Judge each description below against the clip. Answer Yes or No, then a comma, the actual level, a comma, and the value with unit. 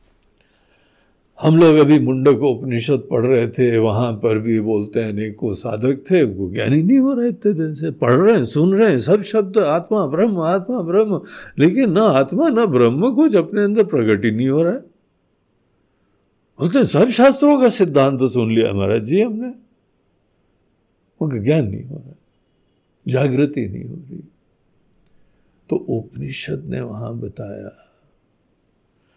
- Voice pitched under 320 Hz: Yes, medium, 140 Hz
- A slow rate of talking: No, average, 150 wpm